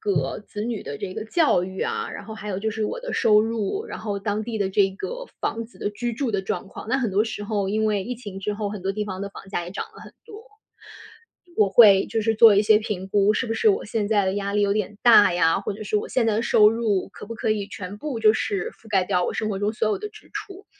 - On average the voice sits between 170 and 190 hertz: No, high, 210 Hz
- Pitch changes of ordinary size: No, narrow, 2.2 semitones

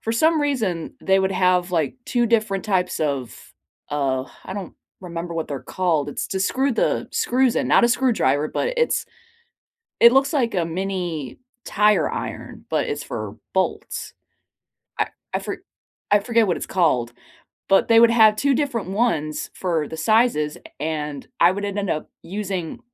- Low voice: No, high, 190 Hz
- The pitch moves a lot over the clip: Yes, wide, 6.1 semitones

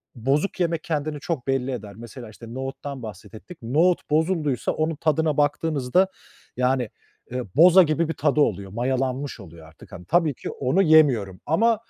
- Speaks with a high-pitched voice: No, medium, 140 Hz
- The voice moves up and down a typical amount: Yes, average, 4.6 semitones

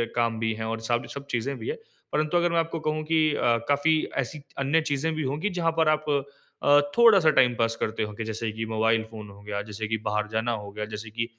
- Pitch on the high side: No, low, 120 Hz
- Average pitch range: No, wide, 5.7 semitones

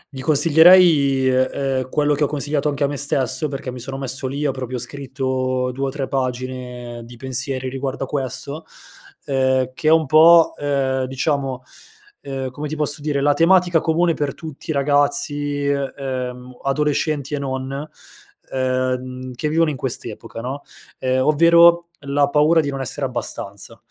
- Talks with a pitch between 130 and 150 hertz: Yes, low, 135 Hz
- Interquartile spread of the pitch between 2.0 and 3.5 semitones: Yes, narrow, 2.4 semitones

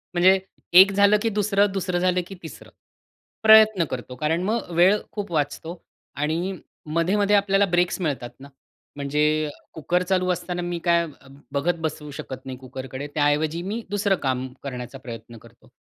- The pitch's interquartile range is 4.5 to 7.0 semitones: Yes, average, 5.1 semitones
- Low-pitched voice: No, medium, 170 Hz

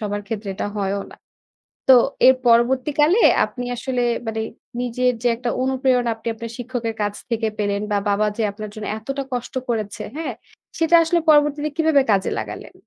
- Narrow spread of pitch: No, average, 3.9 semitones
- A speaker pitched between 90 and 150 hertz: No, high, 240 Hz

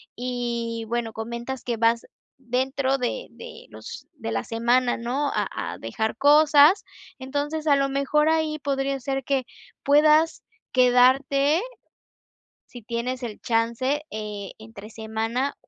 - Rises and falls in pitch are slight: No, average, 3.5 semitones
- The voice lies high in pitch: Yes, very high, 255 Hz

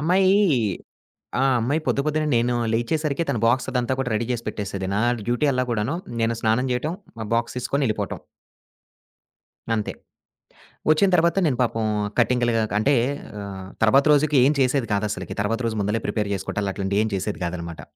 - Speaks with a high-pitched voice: No, low, 120 Hz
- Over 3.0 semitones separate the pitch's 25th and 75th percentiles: Yes, average, 4.7 semitones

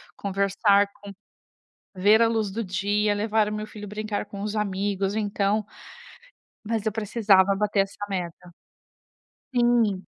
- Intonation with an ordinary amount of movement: No, narrow, 1.4 semitones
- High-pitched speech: Yes, high, 205 Hz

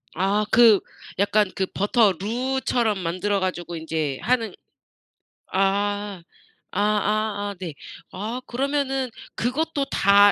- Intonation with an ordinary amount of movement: Yes, average, 3.7 semitones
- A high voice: Yes, high, 205 Hz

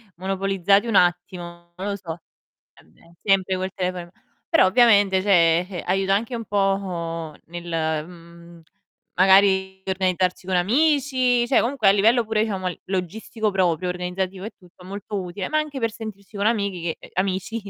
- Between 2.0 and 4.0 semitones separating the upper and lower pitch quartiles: Yes, average, 2.7 semitones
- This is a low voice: No, high, 190 Hz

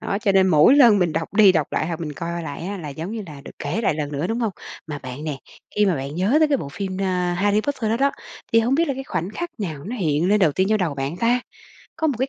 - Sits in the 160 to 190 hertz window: Yes, medium, 185 Hz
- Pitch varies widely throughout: Yes, wide, 6.3 semitones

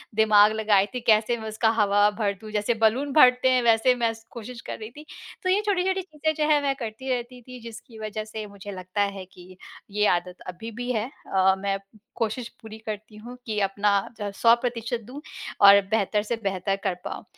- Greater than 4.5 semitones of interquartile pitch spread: No, average, 3.2 semitones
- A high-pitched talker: Yes, high, 220 Hz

